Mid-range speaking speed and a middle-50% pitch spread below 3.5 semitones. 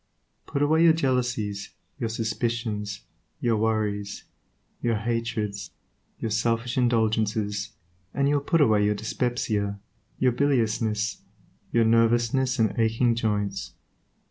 No: slow, 115 wpm; narrow, 2.5 semitones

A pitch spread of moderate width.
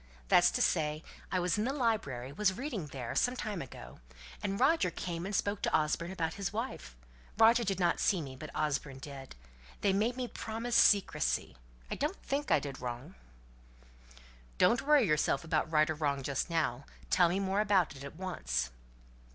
No: wide, 6.7 semitones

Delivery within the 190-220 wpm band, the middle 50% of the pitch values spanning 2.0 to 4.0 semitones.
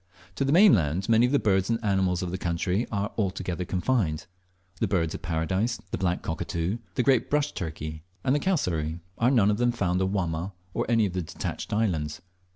No: average, 200 wpm; average, 5.1 semitones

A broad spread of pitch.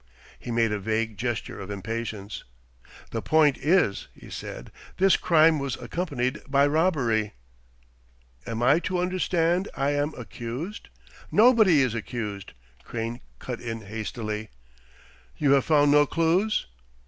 Yes: wide, 6.2 semitones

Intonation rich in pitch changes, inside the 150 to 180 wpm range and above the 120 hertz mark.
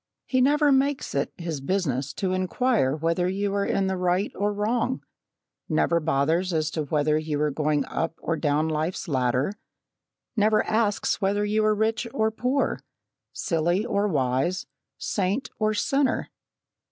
Yes: wide, 5.7 semitones; average, 155 wpm; medium, 185 Hz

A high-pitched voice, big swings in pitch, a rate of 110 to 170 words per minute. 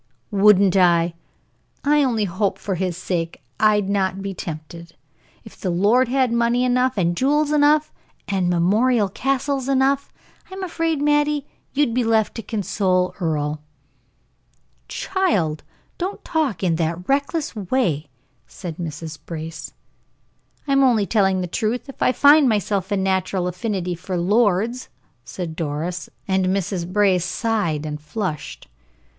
Yes: high, 200 Hz; wide, 6.4 semitones; slow, 135 wpm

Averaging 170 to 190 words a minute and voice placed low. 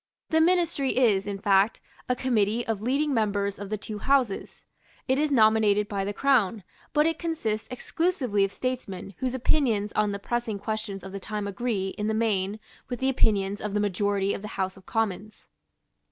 No: average, 185 wpm; high, 215 Hz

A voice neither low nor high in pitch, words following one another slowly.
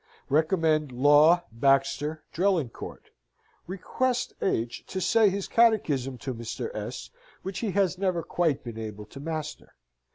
Yes: medium, 160 Hz; slow, 130 wpm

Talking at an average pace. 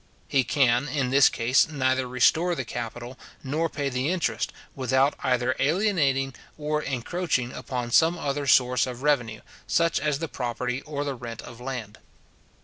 Yes: average, 155 wpm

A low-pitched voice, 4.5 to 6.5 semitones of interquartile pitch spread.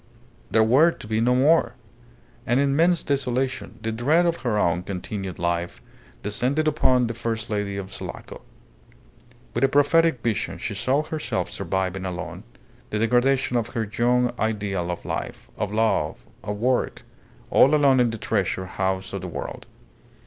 Yes: low, 115 Hz; average, 4.9 semitones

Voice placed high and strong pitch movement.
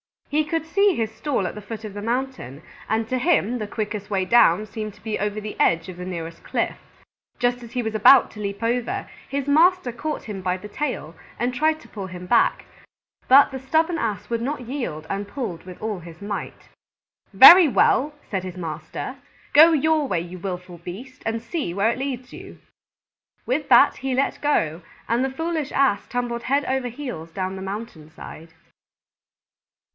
Yes: high, 230 Hz; wide, 5.9 semitones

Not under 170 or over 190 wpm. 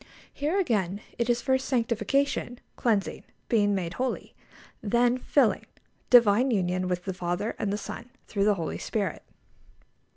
No: average, 140 wpm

